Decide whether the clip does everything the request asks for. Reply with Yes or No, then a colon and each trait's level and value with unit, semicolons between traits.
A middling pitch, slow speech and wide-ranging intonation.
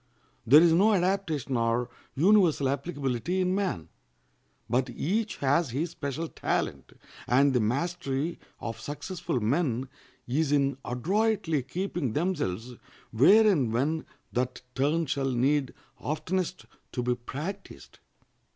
Yes: medium, 145 Hz; slow, 120 wpm; wide, 5.7 semitones